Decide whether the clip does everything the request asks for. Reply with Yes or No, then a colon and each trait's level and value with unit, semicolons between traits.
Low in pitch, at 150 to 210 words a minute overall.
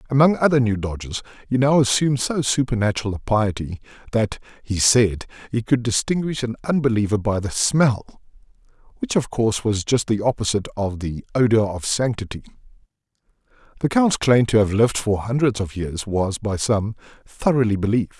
Yes: low, 115 Hz; average, 160 wpm